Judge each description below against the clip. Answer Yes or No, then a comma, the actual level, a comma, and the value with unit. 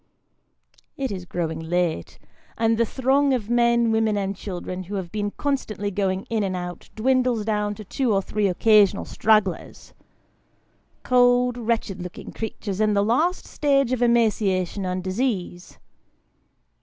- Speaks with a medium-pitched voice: No, high, 215 Hz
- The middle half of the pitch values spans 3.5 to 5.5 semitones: Yes, average, 4.0 semitones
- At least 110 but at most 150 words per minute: Yes, average, 145 wpm